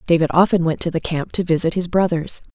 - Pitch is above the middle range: No, medium, 170 Hz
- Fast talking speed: Yes, fast, 235 wpm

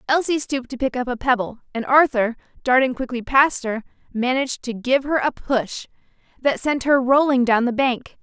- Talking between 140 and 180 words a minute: No, average, 190 wpm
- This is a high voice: Yes, very high, 255 Hz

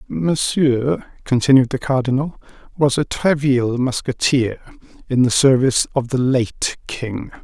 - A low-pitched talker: Yes, low, 130 Hz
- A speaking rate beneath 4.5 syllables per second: Yes, 4.2 syllables/s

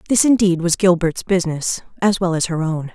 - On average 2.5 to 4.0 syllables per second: No, 5.5 syllables/s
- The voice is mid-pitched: Yes, medium, 175 Hz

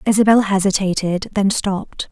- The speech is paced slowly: Yes, slow, 115 wpm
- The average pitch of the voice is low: No, high, 200 Hz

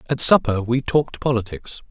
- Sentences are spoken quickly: No, average, 155 wpm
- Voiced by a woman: No, male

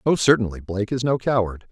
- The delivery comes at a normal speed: No, fast, 210 wpm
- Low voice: Yes, low, 110 Hz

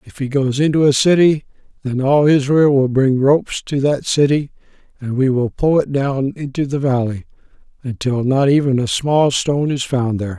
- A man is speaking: Yes, male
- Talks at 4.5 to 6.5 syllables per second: Yes, 5.0 syllables/s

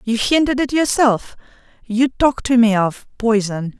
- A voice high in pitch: Yes, high, 235 Hz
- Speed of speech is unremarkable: Yes, average, 160 wpm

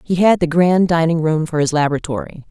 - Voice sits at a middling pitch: Yes, medium, 165 Hz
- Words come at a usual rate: No, fast, 215 wpm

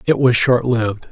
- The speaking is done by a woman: No, male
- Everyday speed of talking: Yes, average, 160 wpm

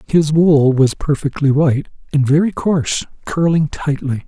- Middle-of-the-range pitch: Yes, medium, 150 Hz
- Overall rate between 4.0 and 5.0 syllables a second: Yes, 4.6 syllables/s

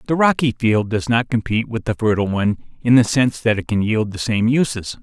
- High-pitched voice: No, low, 115 Hz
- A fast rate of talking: Yes, fast, 240 wpm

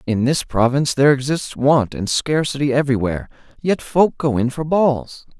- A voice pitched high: No, low, 135 Hz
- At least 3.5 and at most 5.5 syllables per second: Yes, 5.2 syllables/s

